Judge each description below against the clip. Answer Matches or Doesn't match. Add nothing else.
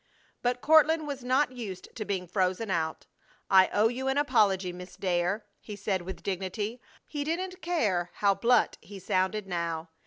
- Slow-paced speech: Doesn't match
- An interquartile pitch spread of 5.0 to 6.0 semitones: Matches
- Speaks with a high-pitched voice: Matches